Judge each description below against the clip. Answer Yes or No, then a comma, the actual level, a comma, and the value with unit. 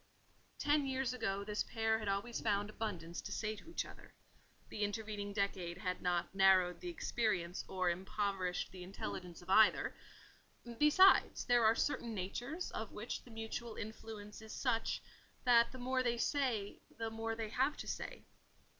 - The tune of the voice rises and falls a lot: No, average, 3.6 semitones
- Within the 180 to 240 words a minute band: No, average, 165 wpm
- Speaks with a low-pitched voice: No, high, 220 Hz